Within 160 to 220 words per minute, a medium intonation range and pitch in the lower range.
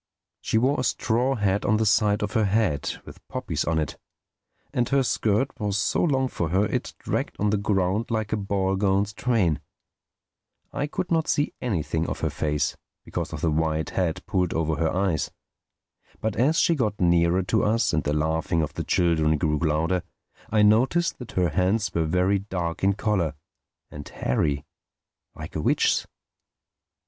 Yes: average, 175 wpm; average, 5.0 semitones; very low, 95 Hz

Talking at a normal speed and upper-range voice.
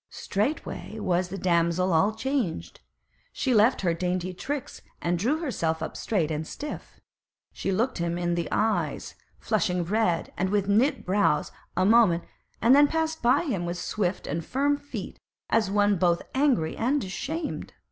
Yes: average, 165 wpm; high, 200 Hz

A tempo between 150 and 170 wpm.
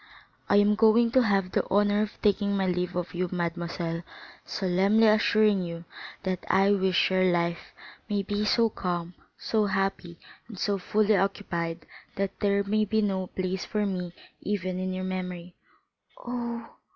Yes: average, 160 wpm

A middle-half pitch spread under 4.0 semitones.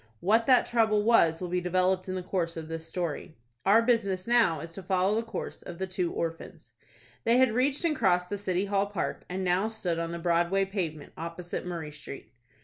Yes: average, 3.6 semitones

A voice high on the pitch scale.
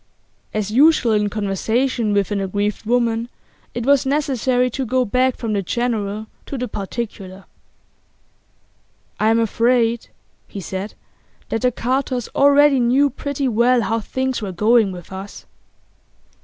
Yes: high, 235 Hz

